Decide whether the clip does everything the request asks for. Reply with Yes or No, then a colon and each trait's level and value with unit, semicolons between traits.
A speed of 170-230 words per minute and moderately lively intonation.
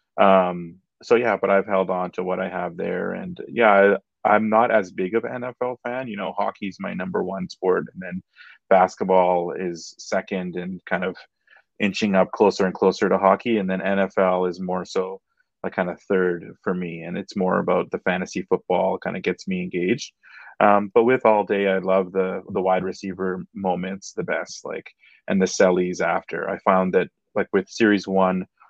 No: average, 200 wpm; narrow, 1.9 semitones